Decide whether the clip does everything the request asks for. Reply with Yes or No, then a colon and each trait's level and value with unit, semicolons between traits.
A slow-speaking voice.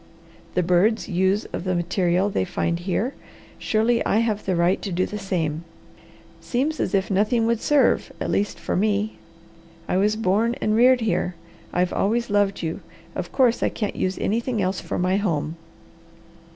No: average, 180 wpm